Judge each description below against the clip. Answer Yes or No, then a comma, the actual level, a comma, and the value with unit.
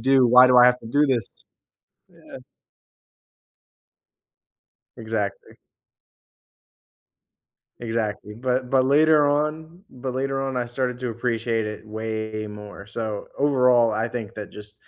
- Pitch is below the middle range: Yes, low, 120 Hz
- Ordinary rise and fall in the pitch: Yes, average, 3.3 semitones